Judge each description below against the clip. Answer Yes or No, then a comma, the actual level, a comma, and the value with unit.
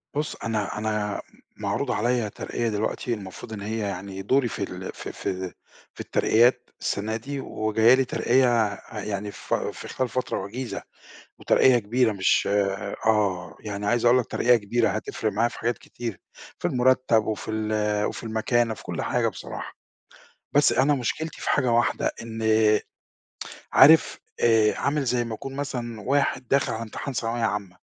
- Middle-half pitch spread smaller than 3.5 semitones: Yes, average, 2.9 semitones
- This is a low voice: Yes, low, 115 Hz